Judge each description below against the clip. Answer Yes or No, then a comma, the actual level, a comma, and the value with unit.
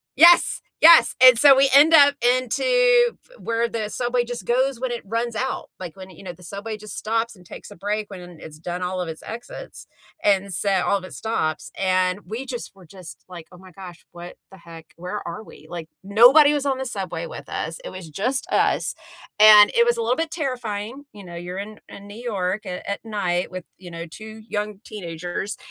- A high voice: Yes, high, 210 Hz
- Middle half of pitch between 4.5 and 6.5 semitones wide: Yes, average, 5.0 semitones